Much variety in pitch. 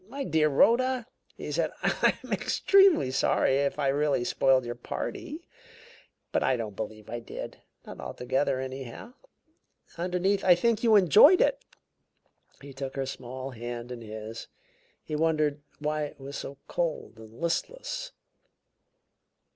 Yes: wide, 6.6 semitones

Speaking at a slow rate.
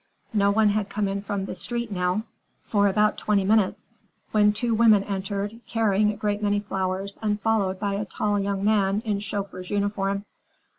No: average, 180 wpm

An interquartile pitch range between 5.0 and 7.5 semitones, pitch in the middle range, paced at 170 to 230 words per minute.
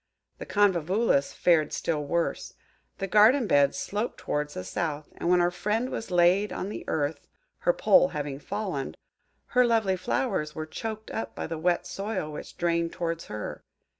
No: wide, 5.5 semitones; medium, 175 Hz; average, 160 wpm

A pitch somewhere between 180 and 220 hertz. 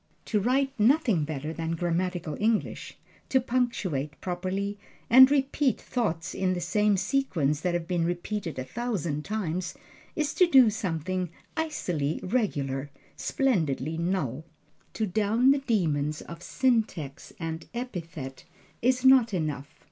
Yes: medium, 185 Hz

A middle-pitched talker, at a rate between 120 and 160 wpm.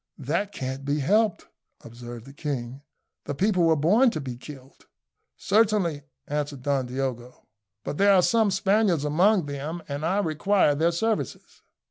Yes: medium, 150 Hz; average, 150 wpm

